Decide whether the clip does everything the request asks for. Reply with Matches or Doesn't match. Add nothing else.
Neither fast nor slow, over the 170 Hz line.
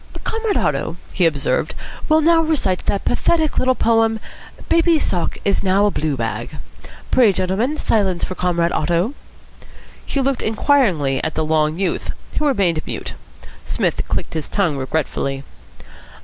Matches